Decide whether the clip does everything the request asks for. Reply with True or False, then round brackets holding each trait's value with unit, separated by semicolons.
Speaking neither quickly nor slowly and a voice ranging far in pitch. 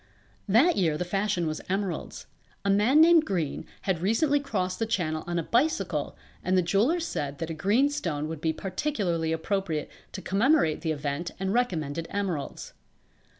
True (165 wpm; 5.9 semitones)